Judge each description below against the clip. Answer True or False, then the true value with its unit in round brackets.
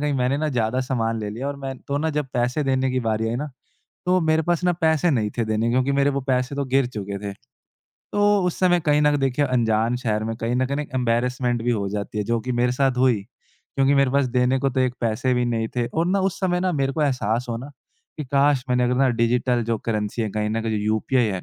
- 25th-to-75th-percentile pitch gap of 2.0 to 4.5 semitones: True (3.5 semitones)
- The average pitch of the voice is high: False (125 Hz)